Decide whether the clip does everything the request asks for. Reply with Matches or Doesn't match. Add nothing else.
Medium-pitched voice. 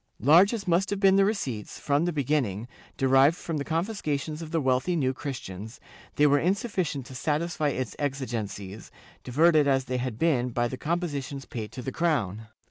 Matches